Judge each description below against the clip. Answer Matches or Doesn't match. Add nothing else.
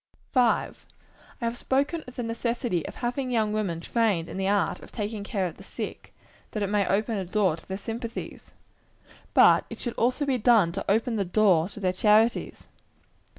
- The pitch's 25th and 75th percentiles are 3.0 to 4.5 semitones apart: Matches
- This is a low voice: Doesn't match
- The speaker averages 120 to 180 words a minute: Doesn't match